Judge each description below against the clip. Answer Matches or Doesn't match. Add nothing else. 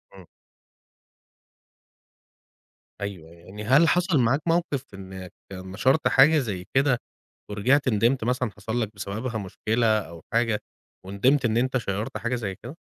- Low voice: Matches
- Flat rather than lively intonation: Doesn't match